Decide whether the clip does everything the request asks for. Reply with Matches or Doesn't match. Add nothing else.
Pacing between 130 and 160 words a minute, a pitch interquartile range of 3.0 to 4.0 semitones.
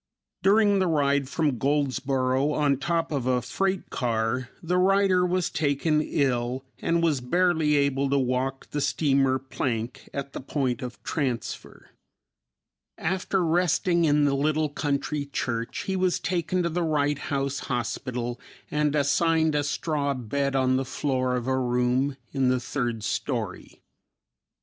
Matches